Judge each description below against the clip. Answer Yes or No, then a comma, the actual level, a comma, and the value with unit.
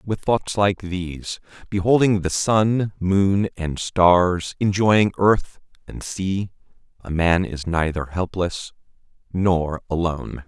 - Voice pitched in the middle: No, very low, 95 Hz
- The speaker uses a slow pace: Yes, slow, 120 wpm